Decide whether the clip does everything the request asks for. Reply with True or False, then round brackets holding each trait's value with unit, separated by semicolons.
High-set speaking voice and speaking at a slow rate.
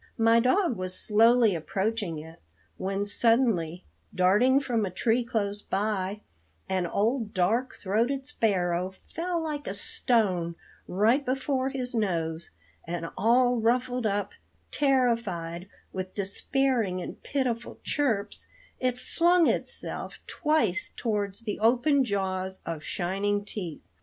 True (215 Hz; 120 wpm)